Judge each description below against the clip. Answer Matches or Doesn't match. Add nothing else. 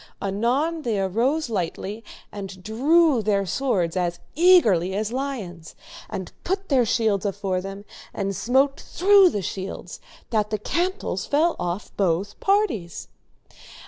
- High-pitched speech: Matches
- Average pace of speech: Doesn't match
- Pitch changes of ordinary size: Doesn't match